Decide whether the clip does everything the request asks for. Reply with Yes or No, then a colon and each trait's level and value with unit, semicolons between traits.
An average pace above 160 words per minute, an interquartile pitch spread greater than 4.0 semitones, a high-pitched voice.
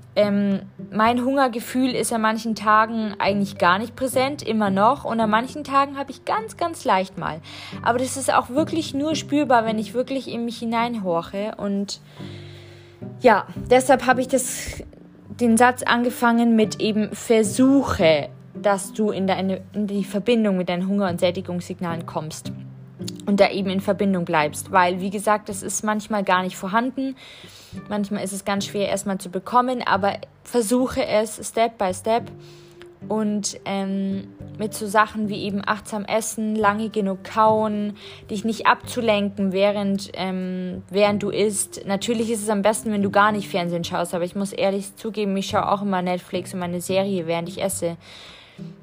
No: average, 170 wpm; average, 3.2 semitones; high, 205 Hz